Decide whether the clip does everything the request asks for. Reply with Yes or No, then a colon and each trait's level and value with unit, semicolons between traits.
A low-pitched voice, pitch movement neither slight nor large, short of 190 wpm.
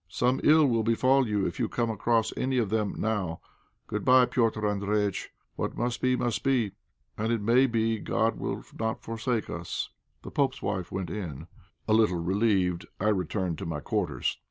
Yes: low, 110 Hz; average, 3.4 semitones; average, 180 wpm